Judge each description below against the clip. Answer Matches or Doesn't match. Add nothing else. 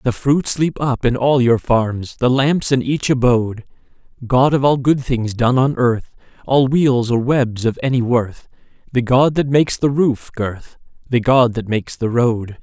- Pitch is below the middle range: Matches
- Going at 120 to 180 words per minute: Doesn't match